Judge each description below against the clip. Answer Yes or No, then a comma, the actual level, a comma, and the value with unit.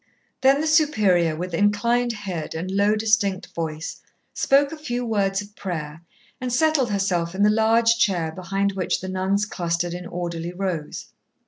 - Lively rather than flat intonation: No, average, 4.4 semitones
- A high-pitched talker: Yes, high, 195 Hz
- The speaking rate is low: No, average, 160 wpm